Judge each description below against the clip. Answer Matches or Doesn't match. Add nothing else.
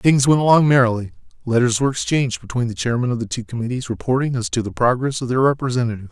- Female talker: Doesn't match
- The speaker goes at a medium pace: Doesn't match